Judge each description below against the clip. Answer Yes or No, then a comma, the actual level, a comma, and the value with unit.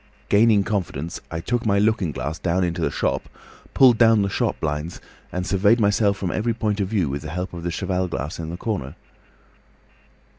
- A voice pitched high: No, very low, 95 Hz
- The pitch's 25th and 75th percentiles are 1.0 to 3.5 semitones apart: No, average, 4.2 semitones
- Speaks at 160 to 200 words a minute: Yes, average, 195 wpm